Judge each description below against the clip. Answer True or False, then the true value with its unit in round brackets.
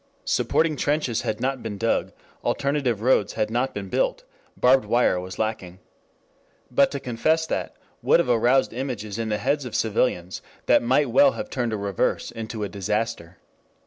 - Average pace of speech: True (170 wpm)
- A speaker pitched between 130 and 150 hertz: False (115 Hz)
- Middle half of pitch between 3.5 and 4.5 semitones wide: True (4.2 semitones)